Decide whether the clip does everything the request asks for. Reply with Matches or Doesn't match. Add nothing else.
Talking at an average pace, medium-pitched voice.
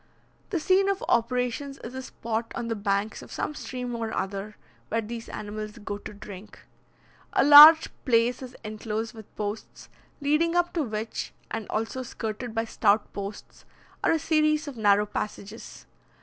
Doesn't match